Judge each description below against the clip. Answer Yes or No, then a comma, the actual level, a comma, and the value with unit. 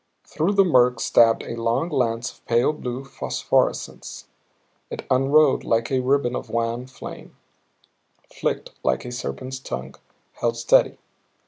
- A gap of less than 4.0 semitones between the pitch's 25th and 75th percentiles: Yes, narrow, 2.5 semitones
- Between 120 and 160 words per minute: Yes, slow, 135 wpm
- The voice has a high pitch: No, low, 125 Hz